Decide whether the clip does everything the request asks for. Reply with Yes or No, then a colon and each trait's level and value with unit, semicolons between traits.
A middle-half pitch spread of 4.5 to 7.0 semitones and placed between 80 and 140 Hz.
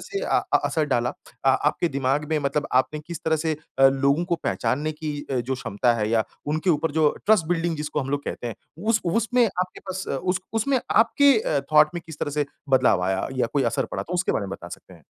No: average, 4.8 semitones; medium, 150 Hz